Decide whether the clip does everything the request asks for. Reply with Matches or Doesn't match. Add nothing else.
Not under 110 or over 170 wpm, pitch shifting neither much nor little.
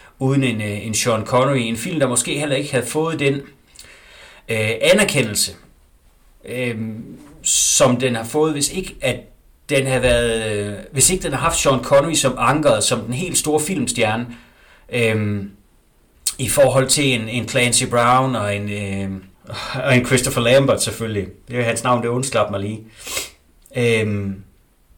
Matches